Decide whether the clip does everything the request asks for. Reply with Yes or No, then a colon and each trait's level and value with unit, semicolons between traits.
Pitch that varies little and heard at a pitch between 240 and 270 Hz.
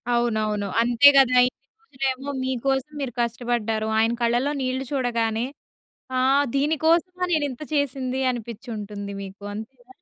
No: average, 3.2 semitones; high, 245 Hz